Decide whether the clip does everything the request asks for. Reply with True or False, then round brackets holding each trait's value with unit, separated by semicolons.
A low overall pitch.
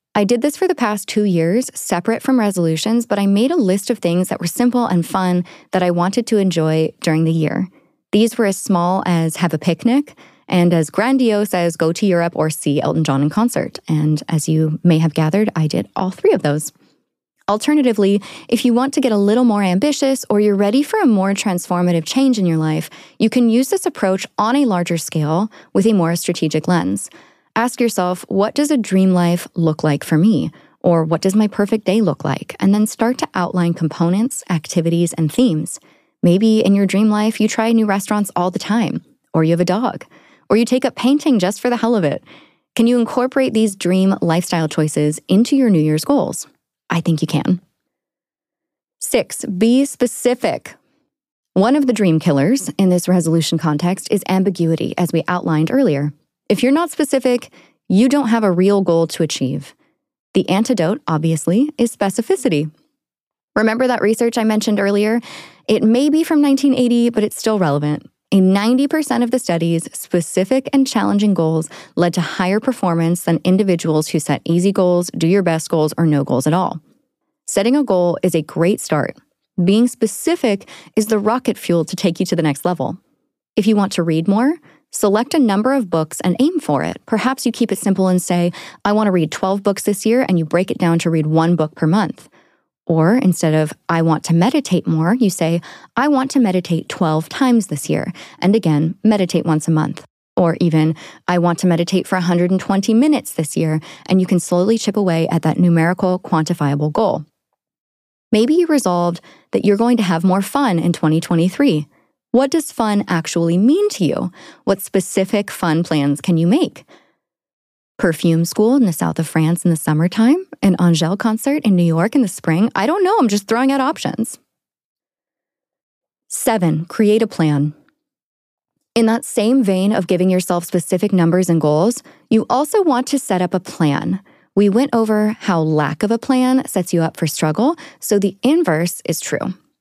False (190 Hz)